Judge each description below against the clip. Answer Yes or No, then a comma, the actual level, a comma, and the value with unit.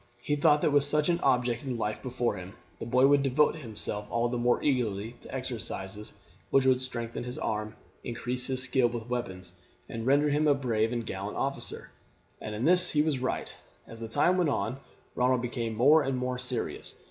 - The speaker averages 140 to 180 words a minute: No, average, 200 wpm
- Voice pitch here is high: No, low, 125 Hz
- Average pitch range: Yes, average, 3.2 semitones